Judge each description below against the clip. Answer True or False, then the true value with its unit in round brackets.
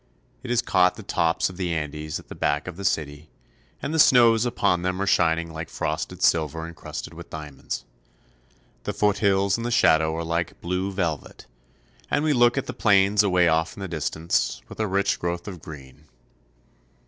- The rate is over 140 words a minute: True (190 wpm)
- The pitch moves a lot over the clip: False (4.0 semitones)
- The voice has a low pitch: True (90 Hz)